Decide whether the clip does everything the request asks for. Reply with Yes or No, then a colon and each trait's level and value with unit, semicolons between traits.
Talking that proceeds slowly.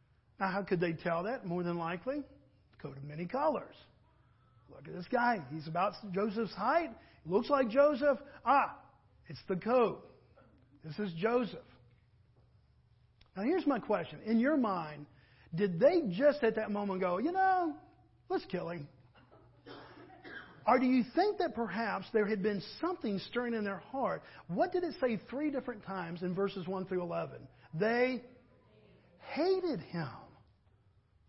No: average, 150 wpm